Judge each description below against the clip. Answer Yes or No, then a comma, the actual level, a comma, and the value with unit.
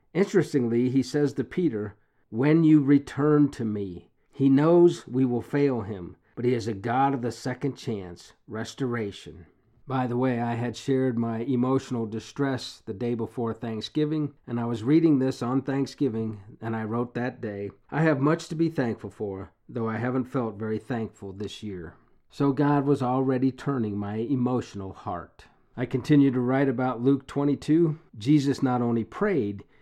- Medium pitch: No, low, 125 Hz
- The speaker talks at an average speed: Yes, average, 170 wpm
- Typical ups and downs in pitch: Yes, average, 3.8 semitones